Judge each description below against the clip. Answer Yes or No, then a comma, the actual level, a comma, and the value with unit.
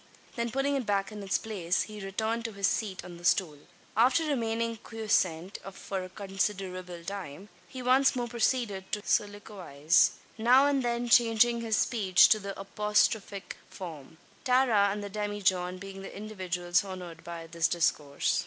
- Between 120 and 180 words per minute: Yes, average, 160 wpm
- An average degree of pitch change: Yes, average, 3.8 semitones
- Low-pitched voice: No, high, 200 Hz